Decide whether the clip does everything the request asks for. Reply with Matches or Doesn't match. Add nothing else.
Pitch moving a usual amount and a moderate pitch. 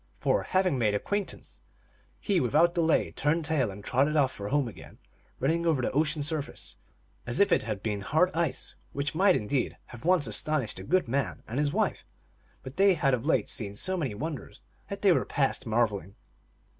Doesn't match